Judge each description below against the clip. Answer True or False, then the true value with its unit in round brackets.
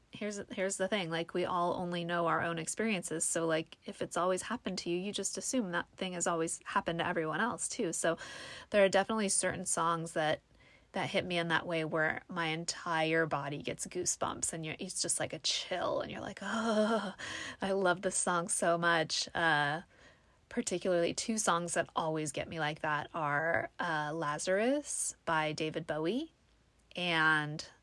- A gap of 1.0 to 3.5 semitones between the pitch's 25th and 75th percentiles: True (3.1 semitones)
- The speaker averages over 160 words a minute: True (185 wpm)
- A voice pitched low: False (170 Hz)